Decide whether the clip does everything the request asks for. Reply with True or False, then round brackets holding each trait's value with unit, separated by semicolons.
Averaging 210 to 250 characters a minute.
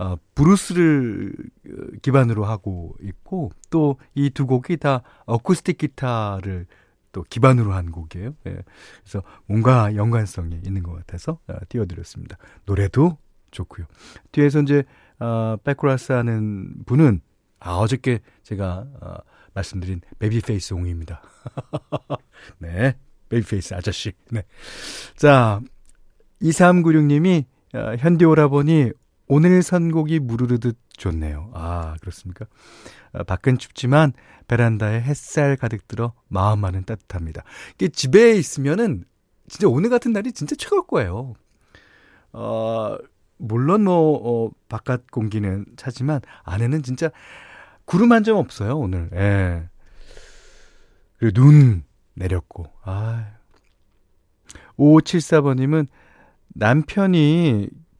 True (240 characters per minute)